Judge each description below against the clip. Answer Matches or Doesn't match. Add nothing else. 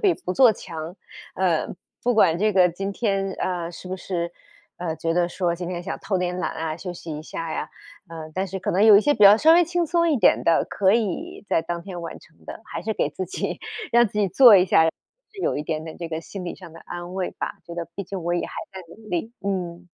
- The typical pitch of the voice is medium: Matches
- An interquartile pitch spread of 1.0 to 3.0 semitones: Doesn't match